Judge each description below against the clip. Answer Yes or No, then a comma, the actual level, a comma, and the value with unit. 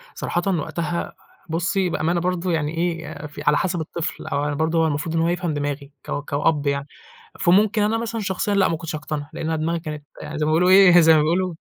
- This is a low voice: No, medium, 165 Hz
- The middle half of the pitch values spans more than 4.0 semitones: No, average, 2.9 semitones